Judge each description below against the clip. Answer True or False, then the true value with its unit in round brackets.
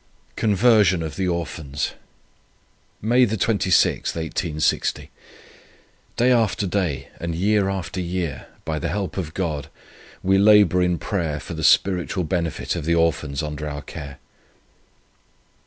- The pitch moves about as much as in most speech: True (3.9 semitones)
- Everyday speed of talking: False (125 wpm)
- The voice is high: False (90 Hz)